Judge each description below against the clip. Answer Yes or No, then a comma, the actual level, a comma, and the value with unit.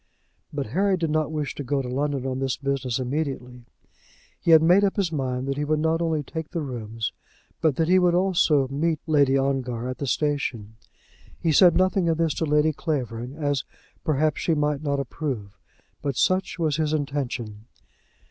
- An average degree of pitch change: Yes, average, 3.4 semitones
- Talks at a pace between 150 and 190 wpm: Yes, average, 185 wpm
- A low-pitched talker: No, medium, 145 Hz